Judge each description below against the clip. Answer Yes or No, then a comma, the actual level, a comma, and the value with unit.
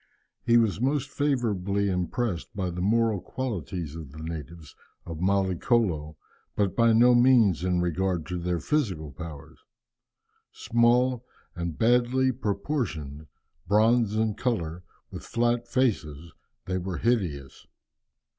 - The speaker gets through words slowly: Yes, slow, 125 wpm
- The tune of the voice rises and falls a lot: Yes, wide, 5.8 semitones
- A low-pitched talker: Yes, low, 100 Hz